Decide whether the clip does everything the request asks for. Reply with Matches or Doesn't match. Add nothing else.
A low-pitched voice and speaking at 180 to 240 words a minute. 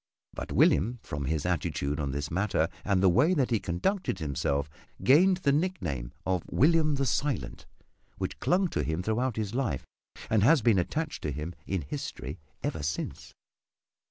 Doesn't match